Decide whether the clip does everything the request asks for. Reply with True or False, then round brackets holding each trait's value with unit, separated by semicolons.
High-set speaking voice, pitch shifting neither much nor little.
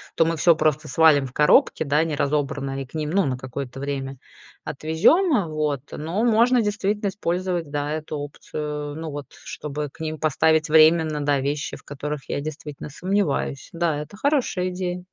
False (155 Hz; 3.3 semitones)